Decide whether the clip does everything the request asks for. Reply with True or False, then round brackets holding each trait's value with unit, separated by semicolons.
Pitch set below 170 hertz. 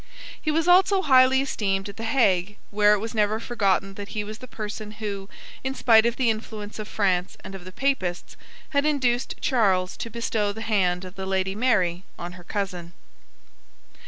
False (210 Hz)